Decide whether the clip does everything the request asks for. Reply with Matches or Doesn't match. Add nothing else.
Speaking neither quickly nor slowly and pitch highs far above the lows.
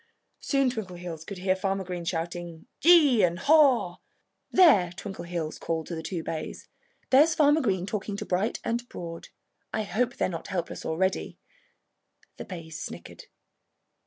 Matches